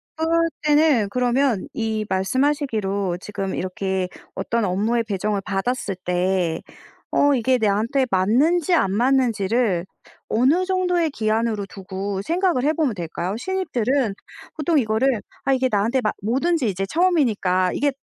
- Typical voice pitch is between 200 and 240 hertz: Yes, high, 230 Hz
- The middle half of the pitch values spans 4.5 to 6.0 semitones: No, wide, 6.4 semitones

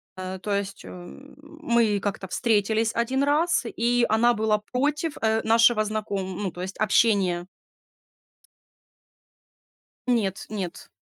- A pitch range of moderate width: Yes, average, 3.4 semitones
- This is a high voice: Yes, high, 220 Hz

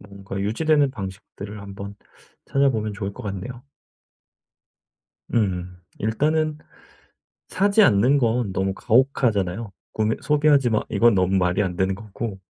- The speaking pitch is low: Yes, low, 105 Hz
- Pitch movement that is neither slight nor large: Yes, average, 4.8 semitones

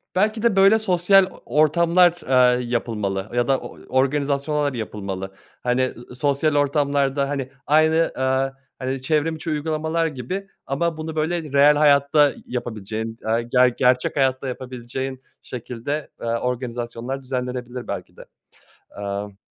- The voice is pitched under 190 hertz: Yes, low, 135 Hz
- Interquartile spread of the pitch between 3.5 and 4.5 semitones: Yes, average, 3.9 semitones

